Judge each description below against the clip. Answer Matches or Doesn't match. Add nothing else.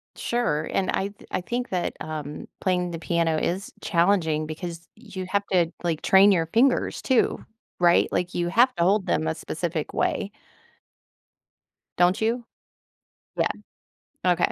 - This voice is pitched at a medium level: Matches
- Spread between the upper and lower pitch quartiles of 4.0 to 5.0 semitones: Doesn't match